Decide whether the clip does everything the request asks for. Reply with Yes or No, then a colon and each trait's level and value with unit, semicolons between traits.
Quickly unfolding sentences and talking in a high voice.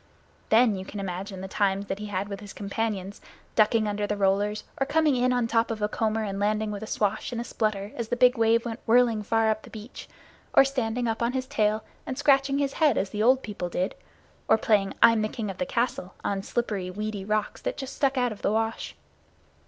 Yes: fast, 230 wpm; high, 215 Hz